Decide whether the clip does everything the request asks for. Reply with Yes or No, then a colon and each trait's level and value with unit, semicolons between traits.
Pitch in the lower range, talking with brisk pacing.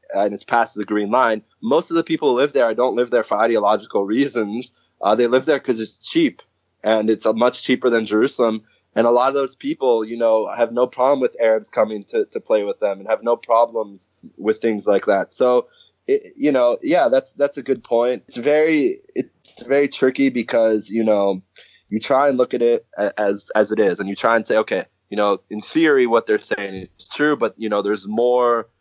Yes: low, 120 Hz; fast, 225 wpm